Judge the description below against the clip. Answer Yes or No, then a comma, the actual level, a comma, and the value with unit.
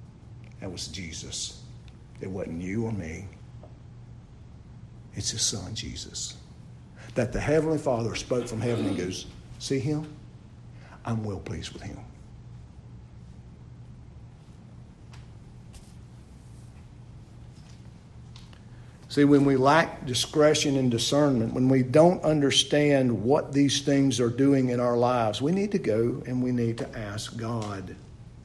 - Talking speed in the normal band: No, slow, 120 wpm